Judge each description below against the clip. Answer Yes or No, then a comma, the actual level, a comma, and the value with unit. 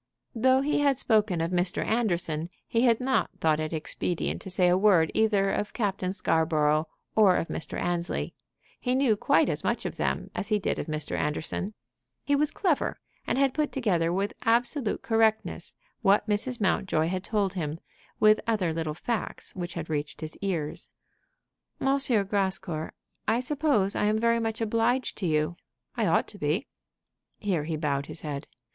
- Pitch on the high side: Yes, high, 195 Hz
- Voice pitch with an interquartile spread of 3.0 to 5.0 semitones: No, wide, 5.6 semitones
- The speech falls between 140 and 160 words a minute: No, average, 175 wpm